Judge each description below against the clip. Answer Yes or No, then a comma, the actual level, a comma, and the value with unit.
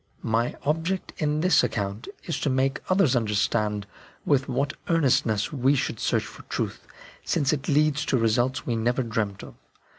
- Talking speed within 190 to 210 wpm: No, average, 160 wpm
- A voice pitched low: Yes, low, 130 Hz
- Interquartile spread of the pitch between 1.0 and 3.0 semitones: No, average, 4.7 semitones